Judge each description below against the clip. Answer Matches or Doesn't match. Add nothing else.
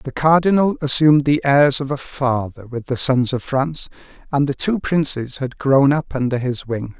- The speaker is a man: Matches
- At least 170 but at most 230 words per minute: Matches